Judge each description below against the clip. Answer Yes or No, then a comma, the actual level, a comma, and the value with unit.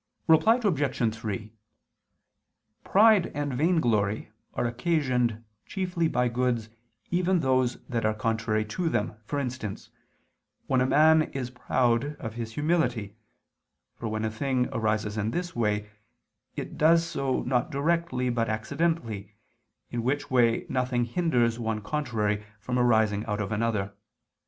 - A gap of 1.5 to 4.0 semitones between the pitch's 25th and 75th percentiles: No, average, 5.0 semitones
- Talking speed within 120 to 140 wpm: Yes, slow, 135 wpm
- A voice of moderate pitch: No, low, 120 Hz